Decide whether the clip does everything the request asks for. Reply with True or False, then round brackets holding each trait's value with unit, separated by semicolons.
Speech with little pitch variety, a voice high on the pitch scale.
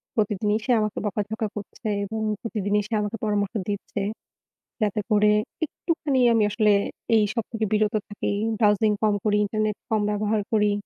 True (1.1 semitones; 210 Hz)